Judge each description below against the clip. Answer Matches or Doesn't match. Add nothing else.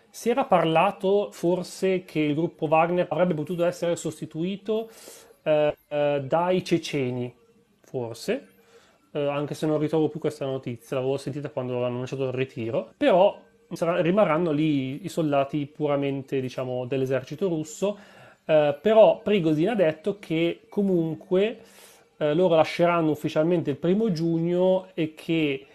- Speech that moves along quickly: Doesn't match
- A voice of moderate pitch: Matches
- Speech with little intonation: Doesn't match